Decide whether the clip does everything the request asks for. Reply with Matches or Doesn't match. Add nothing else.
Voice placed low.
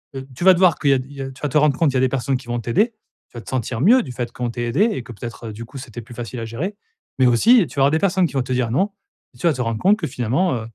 Matches